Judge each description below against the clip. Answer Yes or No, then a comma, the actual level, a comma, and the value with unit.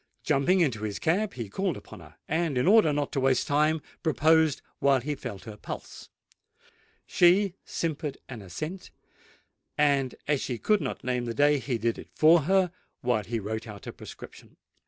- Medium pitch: Yes, medium, 145 Hz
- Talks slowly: No, average, 175 wpm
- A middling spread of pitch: Yes, average, 4.9 semitones